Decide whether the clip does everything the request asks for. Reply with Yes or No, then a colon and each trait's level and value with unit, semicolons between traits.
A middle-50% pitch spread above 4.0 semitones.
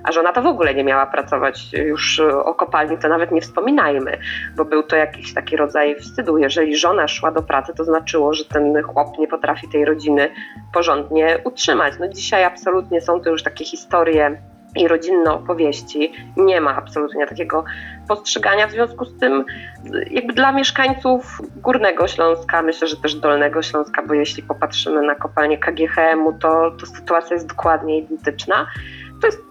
No: narrow, 2.4 semitones